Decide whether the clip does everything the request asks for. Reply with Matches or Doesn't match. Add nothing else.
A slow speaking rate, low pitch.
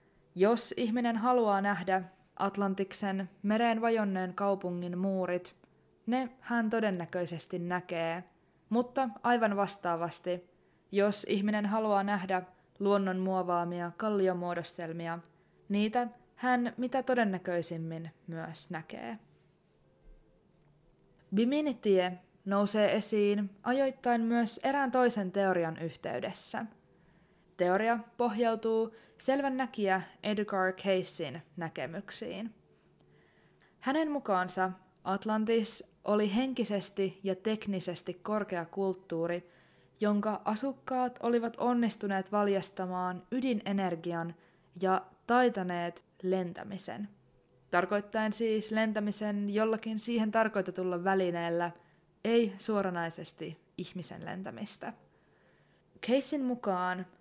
Doesn't match